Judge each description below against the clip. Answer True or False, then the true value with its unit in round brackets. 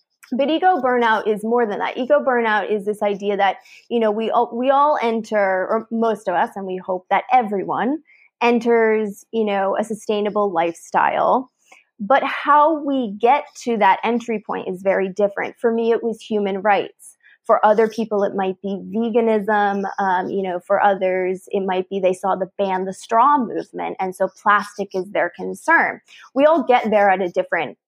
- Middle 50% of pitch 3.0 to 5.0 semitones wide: True (3.3 semitones)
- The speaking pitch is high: True (210 Hz)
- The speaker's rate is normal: True (185 wpm)